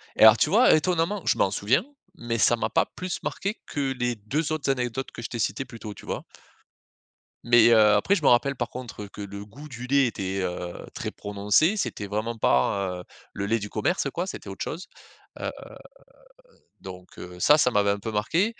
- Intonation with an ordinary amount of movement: No, wide, 5.8 semitones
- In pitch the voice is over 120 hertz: No, low, 115 Hz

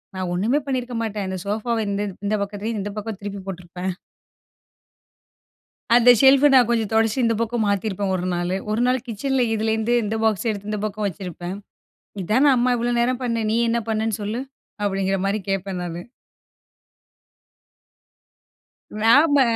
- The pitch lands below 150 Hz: No, high, 215 Hz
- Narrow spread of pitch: No, average, 3.4 semitones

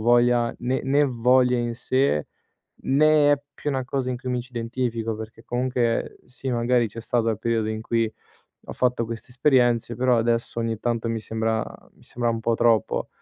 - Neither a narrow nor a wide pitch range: No, narrow, 1.8 semitones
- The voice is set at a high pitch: No, low, 120 Hz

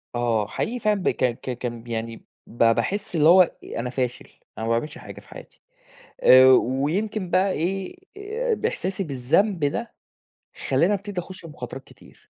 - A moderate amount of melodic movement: No, wide, 8.5 semitones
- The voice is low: No, medium, 165 Hz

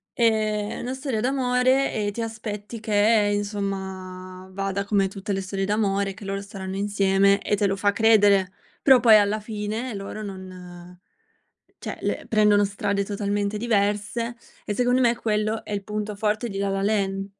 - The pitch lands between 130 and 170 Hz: No, high, 205 Hz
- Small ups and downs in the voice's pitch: Yes, narrow, 1.8 semitones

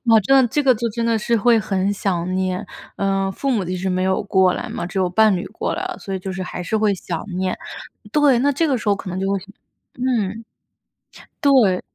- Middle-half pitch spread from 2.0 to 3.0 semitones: No, average, 4.0 semitones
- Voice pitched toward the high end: Yes, high, 200 Hz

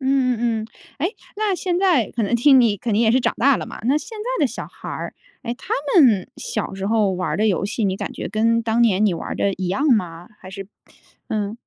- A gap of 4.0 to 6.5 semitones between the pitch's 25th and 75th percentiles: Yes, average, 5.0 semitones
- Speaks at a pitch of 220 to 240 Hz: Yes, high, 230 Hz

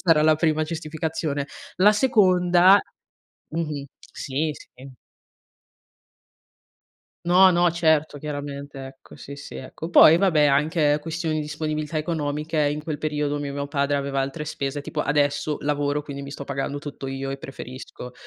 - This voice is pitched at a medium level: Yes, medium, 150 Hz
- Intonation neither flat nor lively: No, narrow, 2.1 semitones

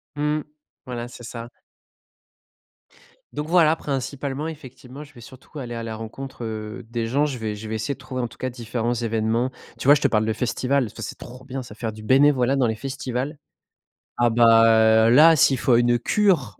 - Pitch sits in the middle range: No, low, 125 Hz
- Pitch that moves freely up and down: No, average, 3.4 semitones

